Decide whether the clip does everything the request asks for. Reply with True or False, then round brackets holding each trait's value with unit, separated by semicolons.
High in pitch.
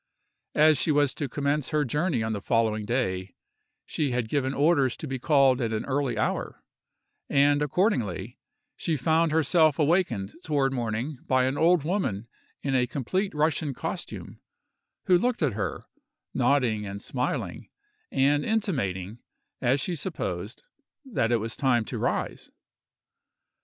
False (135 Hz)